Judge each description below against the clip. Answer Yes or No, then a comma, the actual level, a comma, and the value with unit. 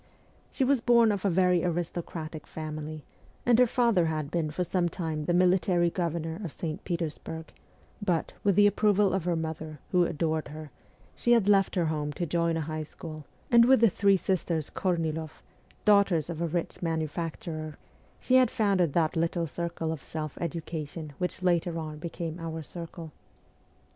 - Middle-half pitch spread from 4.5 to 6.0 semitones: No, narrow, 2.6 semitones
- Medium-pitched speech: Yes, medium, 170 Hz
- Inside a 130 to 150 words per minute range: No, average, 175 wpm